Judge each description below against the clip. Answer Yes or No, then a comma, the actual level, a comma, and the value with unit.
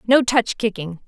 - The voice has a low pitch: No, high, 215 Hz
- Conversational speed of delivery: Yes, average, 165 wpm